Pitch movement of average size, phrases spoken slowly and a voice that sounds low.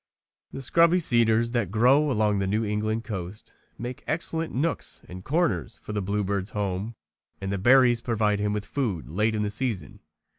No: average, 3.4 semitones; average, 175 wpm; low, 110 Hz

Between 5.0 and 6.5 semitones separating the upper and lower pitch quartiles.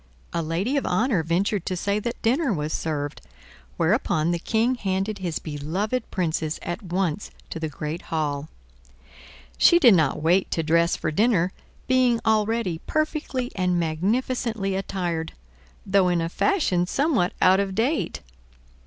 Yes: wide, 5.5 semitones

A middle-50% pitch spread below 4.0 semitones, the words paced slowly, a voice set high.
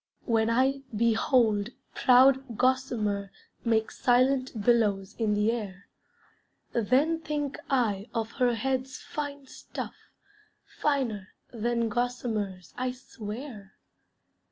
Yes: average, 3.6 semitones; slow, 100 wpm; high, 235 Hz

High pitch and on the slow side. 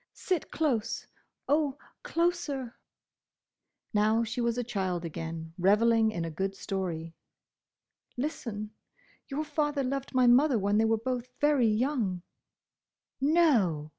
Yes: high, 230 Hz; slow, 120 wpm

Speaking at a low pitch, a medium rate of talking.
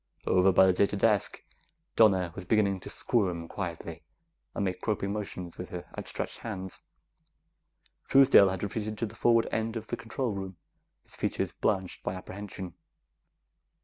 Yes: low, 100 Hz; average, 150 wpm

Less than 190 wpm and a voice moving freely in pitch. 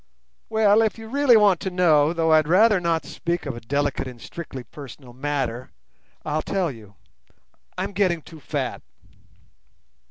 Yes: average, 155 wpm; wide, 5.8 semitones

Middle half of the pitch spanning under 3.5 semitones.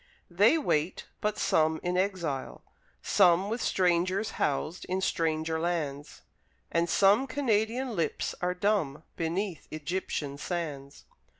No: average, 4.1 semitones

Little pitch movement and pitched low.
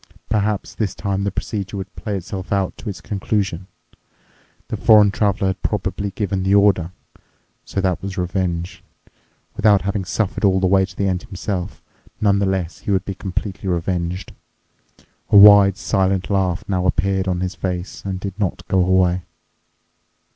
Yes: narrow, 1.5 semitones; very low, 95 Hz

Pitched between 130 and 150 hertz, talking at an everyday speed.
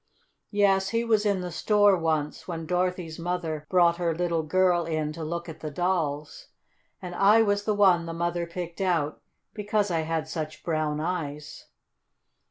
No: medium, 170 Hz; average, 165 wpm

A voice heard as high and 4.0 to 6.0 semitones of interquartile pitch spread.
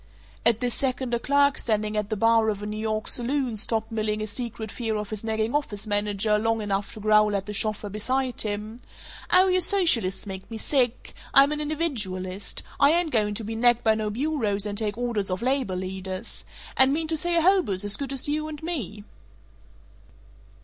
Yes: high, 220 Hz; average, 4.4 semitones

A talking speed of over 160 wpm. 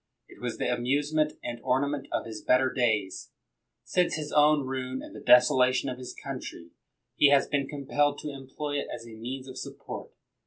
Yes: average, 185 wpm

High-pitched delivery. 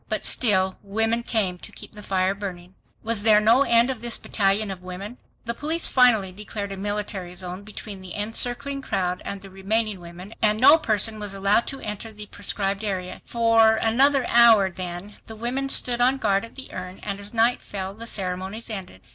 Yes: high, 210 Hz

